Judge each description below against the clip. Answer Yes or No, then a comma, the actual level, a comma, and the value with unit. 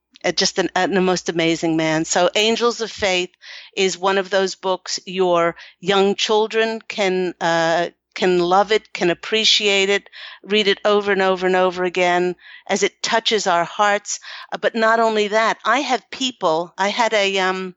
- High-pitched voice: Yes, high, 195 Hz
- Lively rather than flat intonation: No, average, 2.7 semitones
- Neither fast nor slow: Yes, average, 180 wpm